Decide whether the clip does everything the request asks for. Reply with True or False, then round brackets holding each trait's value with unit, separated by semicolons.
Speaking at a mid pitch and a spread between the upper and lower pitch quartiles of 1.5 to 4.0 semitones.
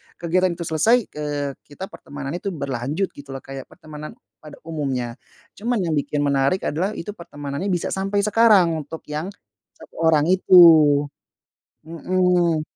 False (160 Hz; 4.4 semitones)